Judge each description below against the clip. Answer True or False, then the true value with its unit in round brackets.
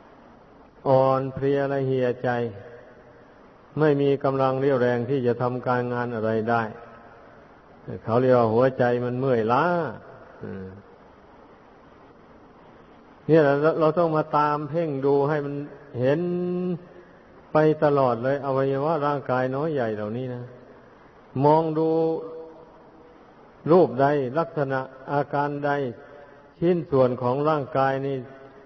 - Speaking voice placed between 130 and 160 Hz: True (135 Hz)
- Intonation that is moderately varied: True (3.3 semitones)